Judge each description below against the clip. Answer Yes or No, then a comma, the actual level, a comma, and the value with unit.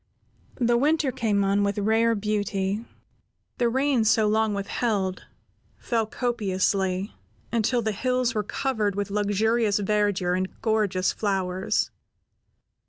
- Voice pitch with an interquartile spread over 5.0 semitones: No, average, 2.7 semitones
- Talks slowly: Yes, slow, 115 wpm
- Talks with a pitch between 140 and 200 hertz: No, high, 210 Hz